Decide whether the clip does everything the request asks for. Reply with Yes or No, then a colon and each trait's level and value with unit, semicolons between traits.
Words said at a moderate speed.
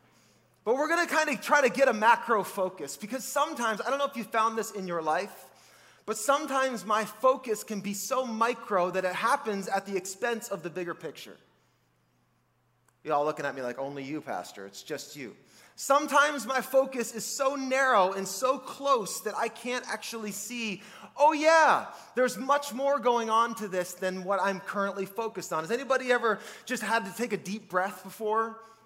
Yes: average, 195 wpm